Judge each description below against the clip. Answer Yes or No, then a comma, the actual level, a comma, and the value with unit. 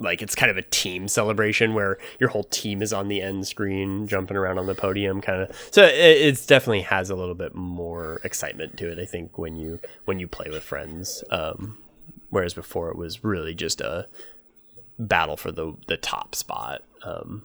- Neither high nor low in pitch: No, very low, 95 Hz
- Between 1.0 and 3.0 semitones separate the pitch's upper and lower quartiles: Yes, average, 2.7 semitones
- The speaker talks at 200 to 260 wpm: Yes, fast, 205 wpm